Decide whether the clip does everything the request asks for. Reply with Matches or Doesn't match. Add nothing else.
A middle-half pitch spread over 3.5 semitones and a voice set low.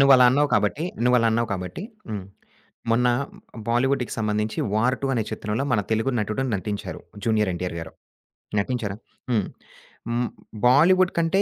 Matches